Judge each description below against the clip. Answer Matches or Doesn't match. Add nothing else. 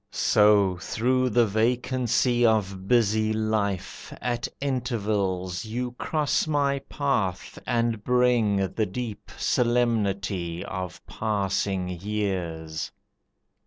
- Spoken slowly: Matches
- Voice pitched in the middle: Doesn't match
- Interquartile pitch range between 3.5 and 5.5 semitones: Matches